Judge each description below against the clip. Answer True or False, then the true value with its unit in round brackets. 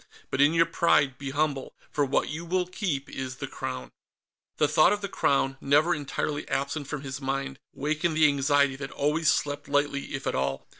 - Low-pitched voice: False (145 Hz)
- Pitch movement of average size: False (2.2 semitones)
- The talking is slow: False (195 wpm)